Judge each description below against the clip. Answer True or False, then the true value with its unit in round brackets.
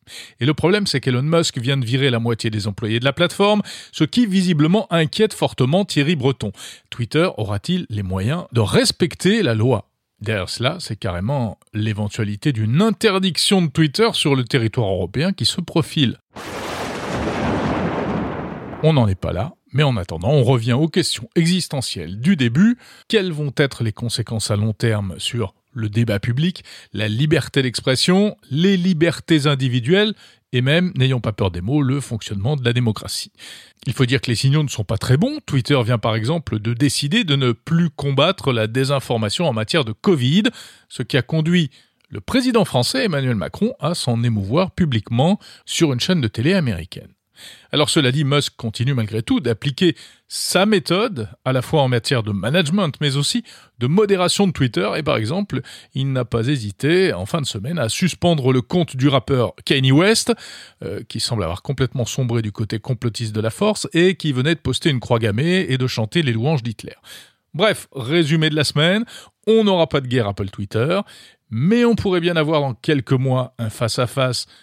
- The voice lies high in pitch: False (135 Hz)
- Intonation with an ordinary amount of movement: False (6.5 semitones)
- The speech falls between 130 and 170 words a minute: False (185 wpm)